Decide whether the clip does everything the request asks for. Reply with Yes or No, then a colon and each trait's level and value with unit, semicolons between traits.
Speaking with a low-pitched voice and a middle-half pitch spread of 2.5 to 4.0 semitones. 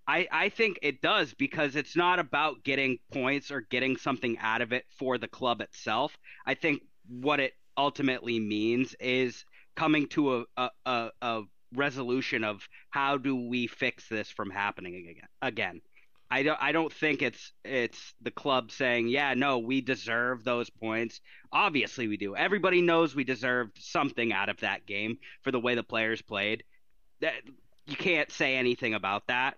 Yes: low, 125 Hz; average, 3.5 semitones